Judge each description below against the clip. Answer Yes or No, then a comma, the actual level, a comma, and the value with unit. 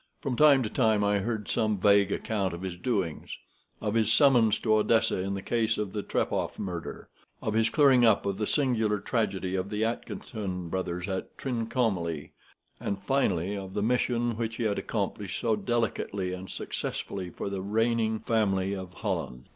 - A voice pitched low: Yes, low, 105 Hz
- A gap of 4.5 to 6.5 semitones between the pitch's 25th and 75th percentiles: No, average, 3.1 semitones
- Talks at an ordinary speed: Yes, average, 175 wpm